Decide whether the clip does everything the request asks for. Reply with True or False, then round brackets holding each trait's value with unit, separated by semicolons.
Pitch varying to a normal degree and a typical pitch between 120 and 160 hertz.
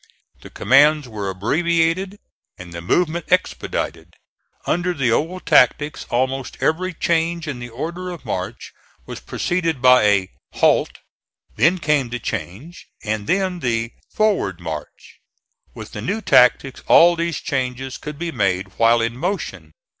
False (7.0 semitones; 135 Hz)